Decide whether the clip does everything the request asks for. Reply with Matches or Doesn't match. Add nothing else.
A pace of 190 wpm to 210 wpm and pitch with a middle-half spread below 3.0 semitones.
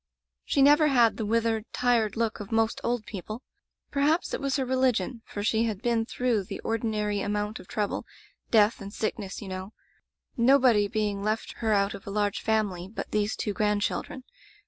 Matches